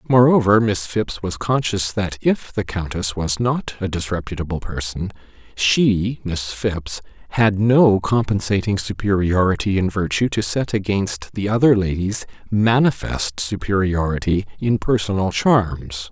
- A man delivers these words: Yes, male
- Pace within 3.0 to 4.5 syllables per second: Yes, 4.2 syllables/s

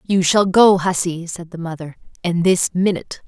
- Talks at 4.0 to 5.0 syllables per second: Yes, 4.9 syllables/s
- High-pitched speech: No, medium, 175 Hz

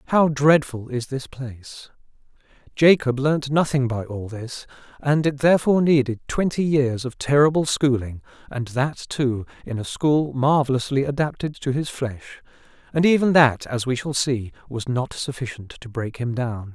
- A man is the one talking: Yes, male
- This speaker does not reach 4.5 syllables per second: No, 4.7 syllables/s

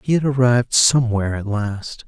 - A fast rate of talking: No, average, 175 wpm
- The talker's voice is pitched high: No, low, 120 Hz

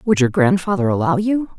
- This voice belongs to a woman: Yes, female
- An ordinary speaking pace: Yes, average, 190 wpm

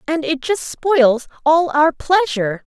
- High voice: Yes, very high, 305 Hz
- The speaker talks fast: No, average, 155 wpm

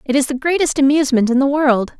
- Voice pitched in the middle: No, very high, 275 Hz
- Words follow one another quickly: Yes, fast, 240 wpm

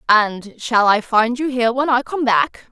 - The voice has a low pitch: No, high, 240 Hz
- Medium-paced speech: No, fast, 220 wpm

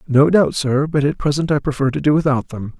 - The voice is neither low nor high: Yes, medium, 145 Hz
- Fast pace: Yes, fast, 260 wpm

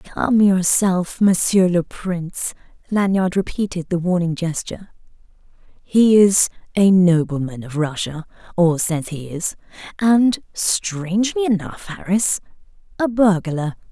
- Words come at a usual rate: No, slow, 105 wpm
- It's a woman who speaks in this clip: Yes, female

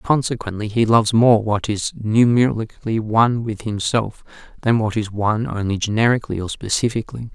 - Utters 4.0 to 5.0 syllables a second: No, 5.7 syllables/s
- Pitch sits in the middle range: No, low, 110 Hz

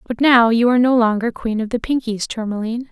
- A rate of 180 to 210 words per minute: No, fast, 225 wpm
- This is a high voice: Yes, high, 235 Hz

